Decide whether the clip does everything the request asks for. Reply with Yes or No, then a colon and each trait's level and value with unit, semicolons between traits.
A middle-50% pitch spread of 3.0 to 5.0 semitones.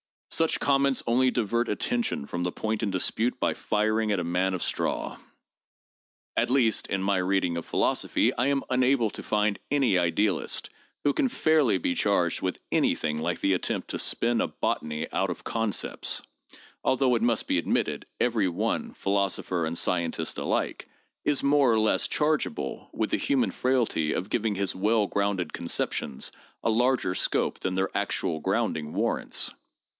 No: wide, 5.4 semitones